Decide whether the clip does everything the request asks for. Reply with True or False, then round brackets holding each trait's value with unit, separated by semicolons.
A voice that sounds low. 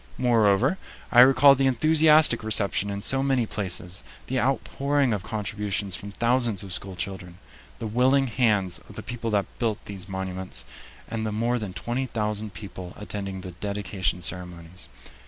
True (105 Hz)